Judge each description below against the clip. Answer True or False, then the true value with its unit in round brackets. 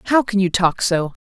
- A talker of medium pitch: False (195 Hz)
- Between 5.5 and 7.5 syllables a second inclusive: False (5.3 syllables/s)